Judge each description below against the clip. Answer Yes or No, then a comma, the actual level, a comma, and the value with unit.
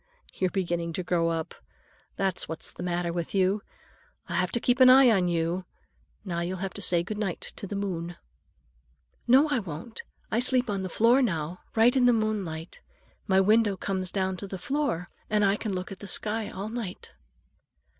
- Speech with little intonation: No, average, 3.8 semitones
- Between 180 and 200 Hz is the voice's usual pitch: Yes, high, 190 Hz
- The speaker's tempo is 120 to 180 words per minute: No, average, 195 wpm